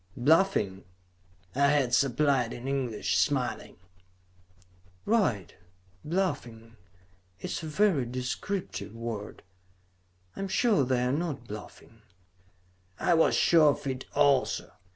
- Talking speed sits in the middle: No, slow, 110 wpm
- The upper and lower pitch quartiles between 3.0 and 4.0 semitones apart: No, wide, 5.4 semitones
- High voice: No, low, 135 Hz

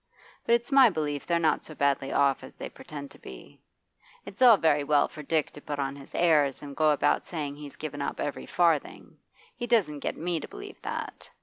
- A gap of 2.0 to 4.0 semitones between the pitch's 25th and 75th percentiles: Yes, average, 3.1 semitones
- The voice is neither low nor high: Yes, medium, 150 Hz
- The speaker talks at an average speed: No, fast, 215 wpm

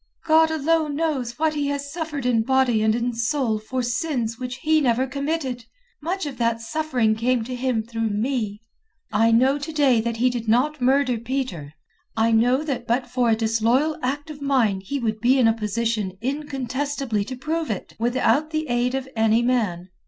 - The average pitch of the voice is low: No, very high, 250 Hz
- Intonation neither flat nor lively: Yes, average, 3.9 semitones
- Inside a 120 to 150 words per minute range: No, average, 190 wpm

